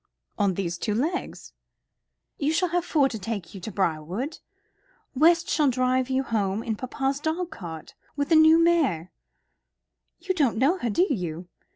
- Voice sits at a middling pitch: No, very high, 260 Hz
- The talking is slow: No, average, 165 wpm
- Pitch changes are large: Yes, wide, 8.2 semitones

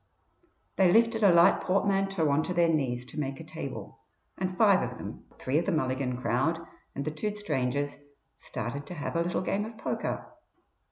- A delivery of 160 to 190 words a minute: Yes, average, 185 wpm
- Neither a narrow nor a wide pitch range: No, wide, 5.7 semitones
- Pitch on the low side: No, medium, 165 Hz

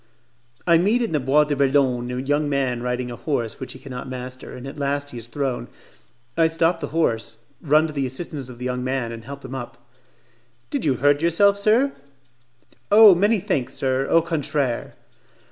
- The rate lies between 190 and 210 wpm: Yes, average, 195 wpm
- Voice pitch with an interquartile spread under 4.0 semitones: No, average, 4.3 semitones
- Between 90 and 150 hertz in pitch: Yes, medium, 140 Hz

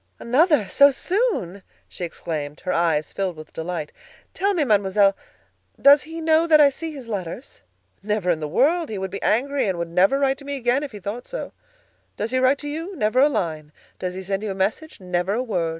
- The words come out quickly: Yes, fast, 215 wpm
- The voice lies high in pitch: Yes, high, 215 Hz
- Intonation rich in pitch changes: Yes, wide, 7.7 semitones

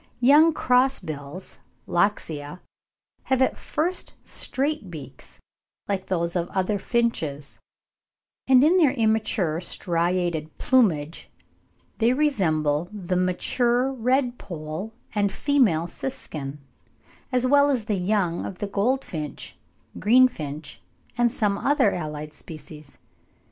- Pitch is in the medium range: No, high, 200 Hz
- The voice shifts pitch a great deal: Yes, wide, 7.9 semitones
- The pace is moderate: No, slow, 110 wpm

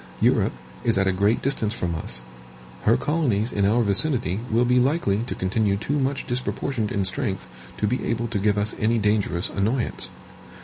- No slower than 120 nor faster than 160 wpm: No, average, 180 wpm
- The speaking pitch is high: No, low, 110 Hz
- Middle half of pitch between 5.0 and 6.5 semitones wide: No, average, 3.8 semitones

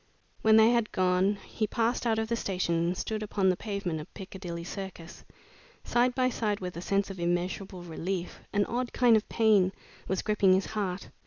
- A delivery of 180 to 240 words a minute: Yes, average, 190 wpm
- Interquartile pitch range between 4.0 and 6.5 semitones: No, average, 3.2 semitones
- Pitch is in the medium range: No, high, 195 Hz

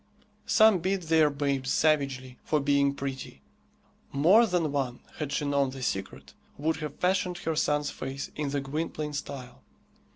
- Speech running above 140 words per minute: Yes, average, 155 wpm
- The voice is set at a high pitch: No, medium, 145 Hz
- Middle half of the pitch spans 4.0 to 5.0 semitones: No, narrow, 2.6 semitones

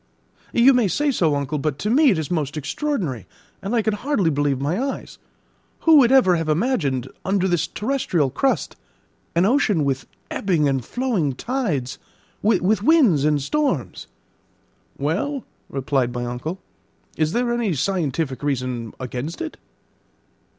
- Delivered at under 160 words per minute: Yes, average, 145 wpm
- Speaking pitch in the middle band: Yes, medium, 170 Hz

